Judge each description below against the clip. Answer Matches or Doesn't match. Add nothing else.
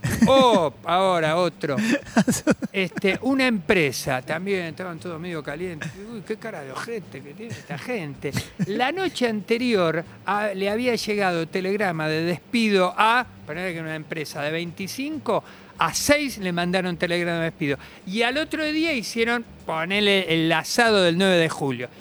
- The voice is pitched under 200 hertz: Matches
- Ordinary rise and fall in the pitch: Doesn't match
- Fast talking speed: Doesn't match